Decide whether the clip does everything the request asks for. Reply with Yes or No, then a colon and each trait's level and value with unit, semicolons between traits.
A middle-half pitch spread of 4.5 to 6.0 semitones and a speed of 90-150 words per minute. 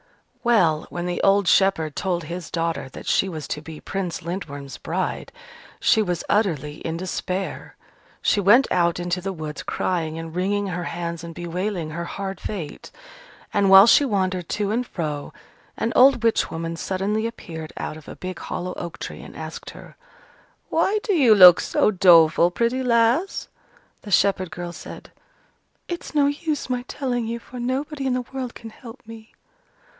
No: average, 5.3 semitones; average, 170 wpm